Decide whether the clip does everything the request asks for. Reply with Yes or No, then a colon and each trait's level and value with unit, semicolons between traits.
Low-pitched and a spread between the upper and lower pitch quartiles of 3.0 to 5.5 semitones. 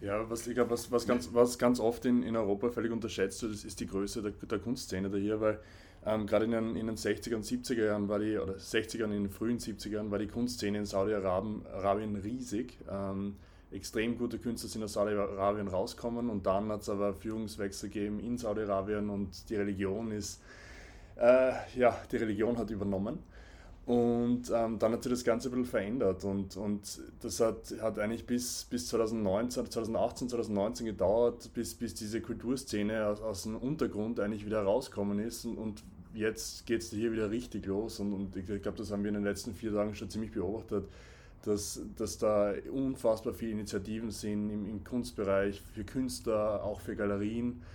No: low, 105 Hz; narrow, 2.4 semitones